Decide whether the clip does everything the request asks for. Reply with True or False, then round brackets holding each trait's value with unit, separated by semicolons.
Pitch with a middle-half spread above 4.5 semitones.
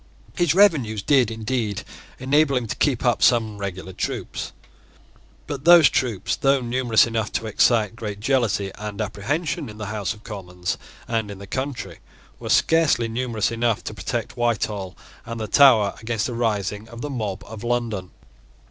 False (3.7 semitones)